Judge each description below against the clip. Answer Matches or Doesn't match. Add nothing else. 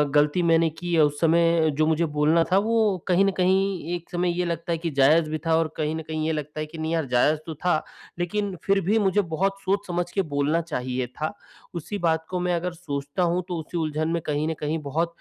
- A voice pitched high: Doesn't match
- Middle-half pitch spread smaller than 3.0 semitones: Matches